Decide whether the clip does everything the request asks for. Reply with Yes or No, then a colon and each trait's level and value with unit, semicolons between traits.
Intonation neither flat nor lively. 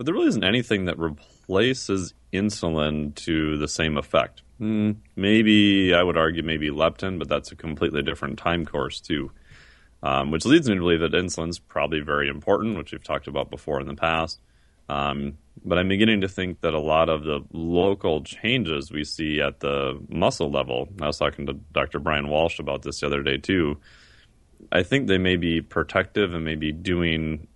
Yes: average, 3.8 semitones